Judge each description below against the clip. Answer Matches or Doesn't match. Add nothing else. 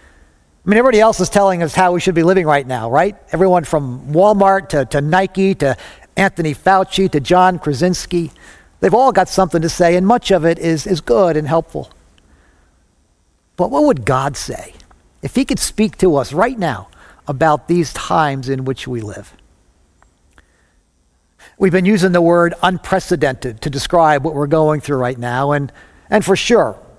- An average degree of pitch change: Doesn't match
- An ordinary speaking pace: Matches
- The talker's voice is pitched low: Doesn't match